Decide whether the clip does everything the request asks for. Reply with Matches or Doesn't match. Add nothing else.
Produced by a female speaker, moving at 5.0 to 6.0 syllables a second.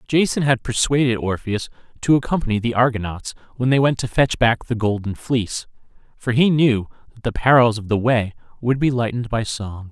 Doesn't match